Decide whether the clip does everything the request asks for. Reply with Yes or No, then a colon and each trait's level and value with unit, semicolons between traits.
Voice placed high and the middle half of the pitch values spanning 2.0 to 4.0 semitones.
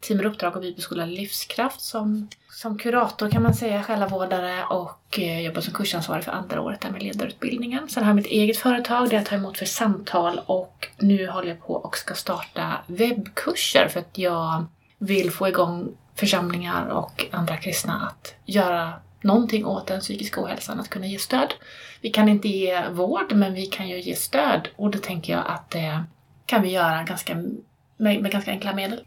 Yes: high, 200 Hz; average, 3.0 semitones